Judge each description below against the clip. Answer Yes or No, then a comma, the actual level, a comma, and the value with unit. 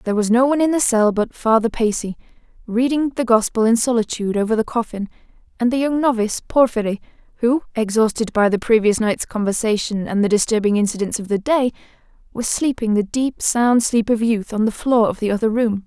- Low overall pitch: No, high, 225 Hz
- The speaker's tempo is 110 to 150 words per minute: No, average, 195 wpm